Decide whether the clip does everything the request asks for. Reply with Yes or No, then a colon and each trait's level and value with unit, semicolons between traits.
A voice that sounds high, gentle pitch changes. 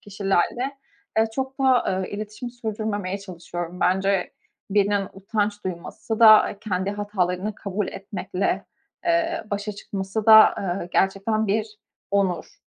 Yes: high, 205 Hz; narrow, 2.2 semitones